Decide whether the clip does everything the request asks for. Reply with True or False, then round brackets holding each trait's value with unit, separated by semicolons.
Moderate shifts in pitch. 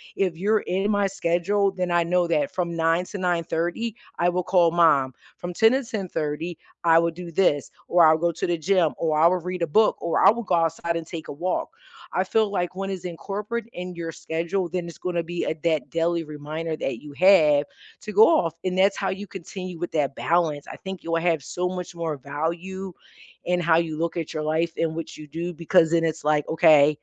False (2.3 semitones)